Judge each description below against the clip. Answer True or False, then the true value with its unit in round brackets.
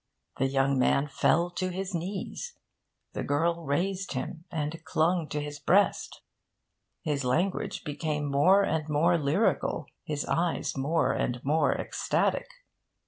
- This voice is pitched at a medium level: True (155 Hz)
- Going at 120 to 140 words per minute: True (135 wpm)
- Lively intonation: False (3.4 semitones)